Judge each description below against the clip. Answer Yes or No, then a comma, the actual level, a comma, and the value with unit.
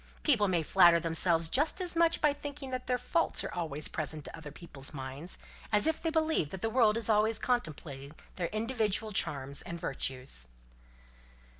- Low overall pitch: No, high, 190 Hz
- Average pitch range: No, wide, 8.3 semitones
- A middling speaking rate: Yes, average, 175 wpm